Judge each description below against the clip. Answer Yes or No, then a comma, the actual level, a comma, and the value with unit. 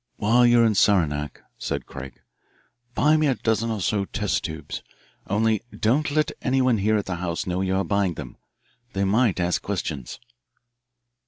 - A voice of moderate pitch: No, low, 100 Hz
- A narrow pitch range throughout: No, average, 4.4 semitones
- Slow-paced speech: No, average, 165 wpm